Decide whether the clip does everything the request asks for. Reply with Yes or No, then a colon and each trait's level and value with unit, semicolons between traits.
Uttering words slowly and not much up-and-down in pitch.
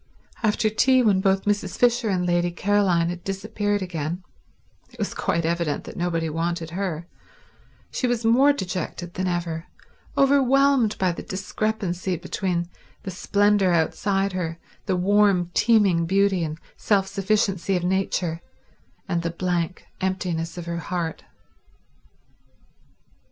No: slow, 125 wpm; average, 3.1 semitones